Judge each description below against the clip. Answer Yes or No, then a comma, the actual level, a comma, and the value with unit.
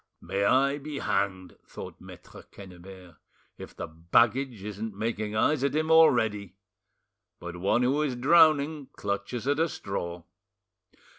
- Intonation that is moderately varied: No, wide, 6.3 semitones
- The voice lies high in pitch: No, low, 110 Hz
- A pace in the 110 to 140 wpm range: Yes, slow, 135 wpm